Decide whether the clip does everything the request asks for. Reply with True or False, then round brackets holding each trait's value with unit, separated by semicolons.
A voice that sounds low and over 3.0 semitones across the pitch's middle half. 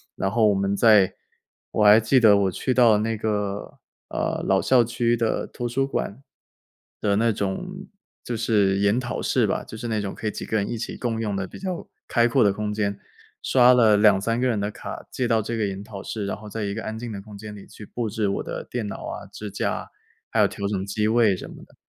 False (110 Hz; 2.6 semitones)